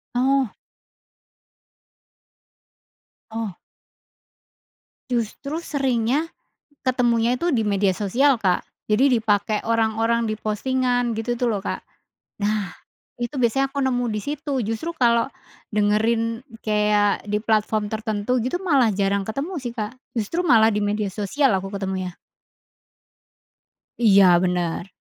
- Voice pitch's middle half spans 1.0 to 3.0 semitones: No, average, 3.4 semitones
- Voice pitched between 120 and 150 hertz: No, high, 225 Hz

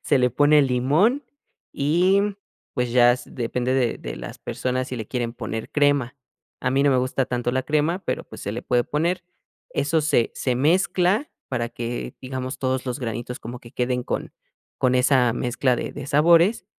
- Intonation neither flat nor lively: Yes, average, 3.1 semitones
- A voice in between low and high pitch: No, low, 130 Hz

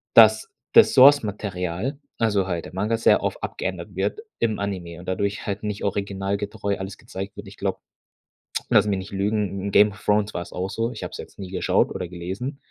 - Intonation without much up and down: Yes, narrow, 1.9 semitones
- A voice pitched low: Yes, low, 100 Hz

